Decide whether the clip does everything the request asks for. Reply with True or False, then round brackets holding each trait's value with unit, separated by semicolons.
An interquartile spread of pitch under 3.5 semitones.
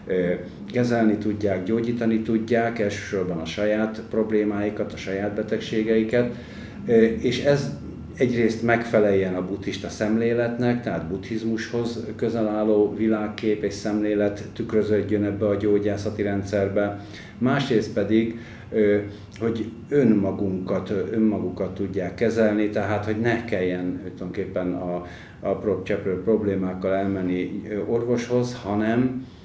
True (2.4 semitones)